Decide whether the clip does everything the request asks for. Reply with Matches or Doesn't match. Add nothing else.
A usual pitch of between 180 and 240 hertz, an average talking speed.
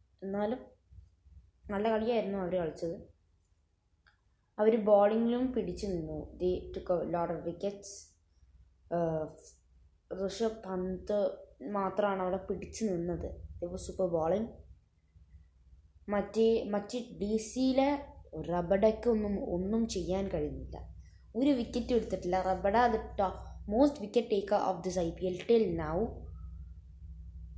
Matches